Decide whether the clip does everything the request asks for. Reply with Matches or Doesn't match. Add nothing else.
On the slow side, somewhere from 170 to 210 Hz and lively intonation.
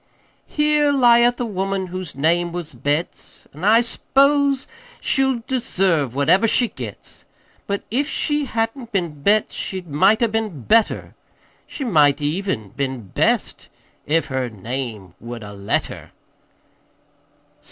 Matches